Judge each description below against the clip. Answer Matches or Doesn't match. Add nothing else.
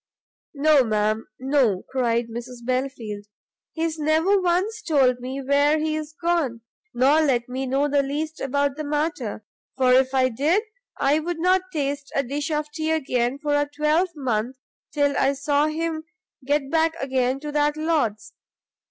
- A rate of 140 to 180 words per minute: Matches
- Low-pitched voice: Doesn't match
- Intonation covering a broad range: Doesn't match